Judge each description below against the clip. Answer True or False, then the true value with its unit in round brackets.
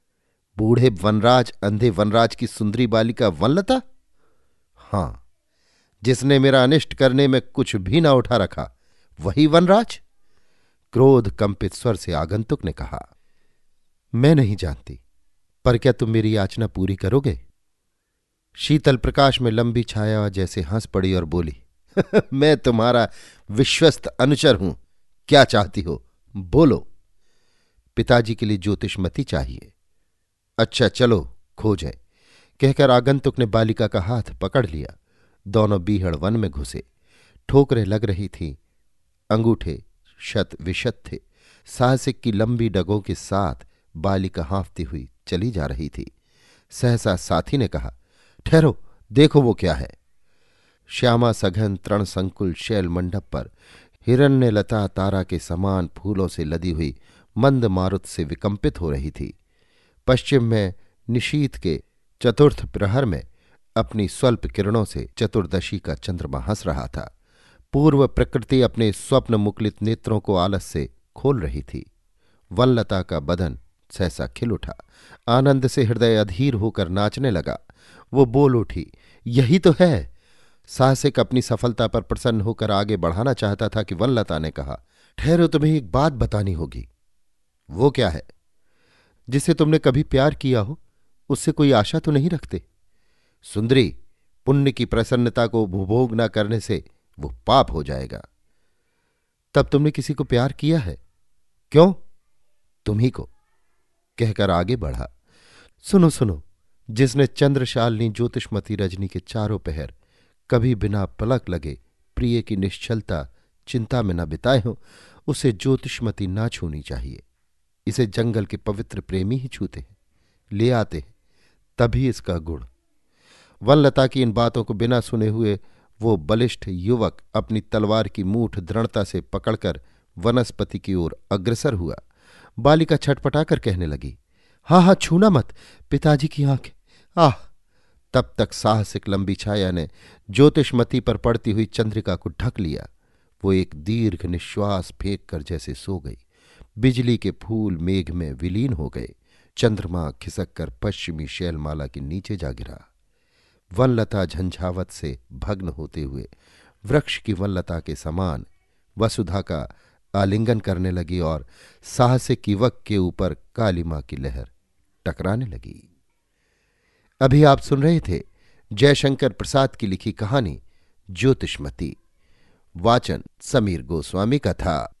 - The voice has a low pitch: True (105 Hz)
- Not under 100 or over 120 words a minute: False (135 wpm)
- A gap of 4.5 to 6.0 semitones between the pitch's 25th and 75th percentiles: True (5.6 semitones)